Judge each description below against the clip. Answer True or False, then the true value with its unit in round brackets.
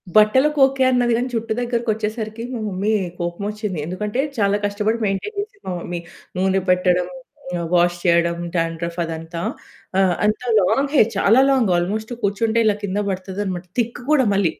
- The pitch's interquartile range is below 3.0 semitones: False (4.2 semitones)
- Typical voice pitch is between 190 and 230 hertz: True (205 Hz)